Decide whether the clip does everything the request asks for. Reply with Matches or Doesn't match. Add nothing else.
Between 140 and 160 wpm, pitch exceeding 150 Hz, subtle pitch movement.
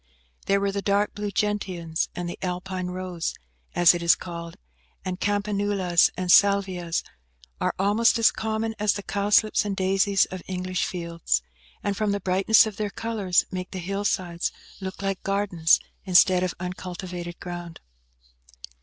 Matches